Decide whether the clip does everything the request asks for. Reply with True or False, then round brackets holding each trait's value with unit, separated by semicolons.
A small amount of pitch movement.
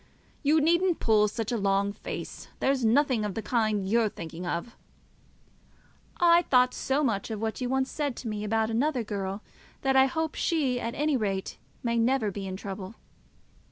False (4.5 semitones)